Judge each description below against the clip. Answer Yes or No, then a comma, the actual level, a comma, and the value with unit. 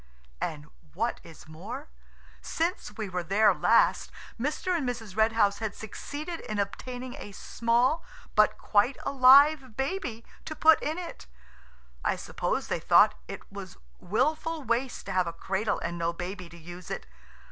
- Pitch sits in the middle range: No, high, 225 Hz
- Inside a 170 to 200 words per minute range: No, average, 160 wpm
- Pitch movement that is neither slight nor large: No, wide, 6.6 semitones